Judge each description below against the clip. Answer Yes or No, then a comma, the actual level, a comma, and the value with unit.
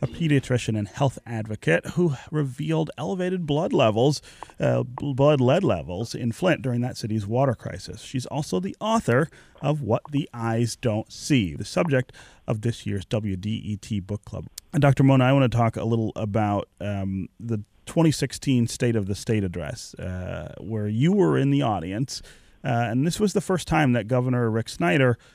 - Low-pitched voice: Yes, low, 120 Hz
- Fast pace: No, average, 180 wpm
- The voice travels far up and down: No, average, 4.7 semitones